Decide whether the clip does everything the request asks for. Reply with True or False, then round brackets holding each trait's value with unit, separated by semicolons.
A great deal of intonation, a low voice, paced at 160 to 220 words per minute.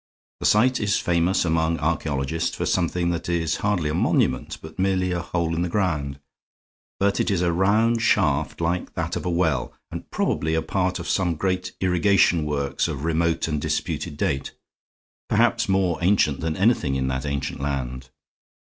False (3.4 semitones; 85 Hz; 175 wpm)